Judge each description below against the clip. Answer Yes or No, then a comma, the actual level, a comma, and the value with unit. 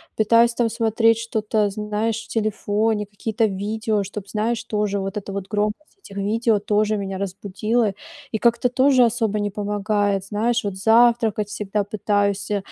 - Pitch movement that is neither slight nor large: No, narrow, 1.9 semitones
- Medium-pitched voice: No, high, 210 Hz